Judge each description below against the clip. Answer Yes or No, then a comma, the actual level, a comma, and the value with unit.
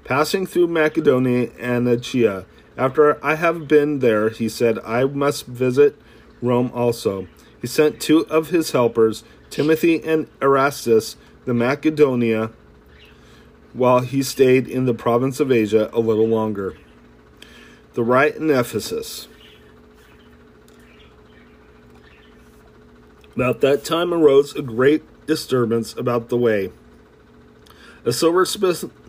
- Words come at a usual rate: No, slow, 115 wpm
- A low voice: Yes, low, 120 Hz